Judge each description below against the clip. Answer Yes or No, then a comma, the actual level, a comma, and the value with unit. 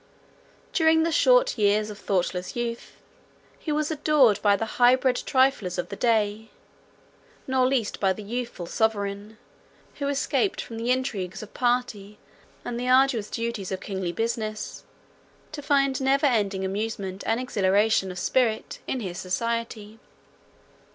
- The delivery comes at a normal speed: Yes, average, 145 wpm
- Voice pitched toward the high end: Yes, high, 225 Hz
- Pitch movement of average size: Yes, average, 4.3 semitones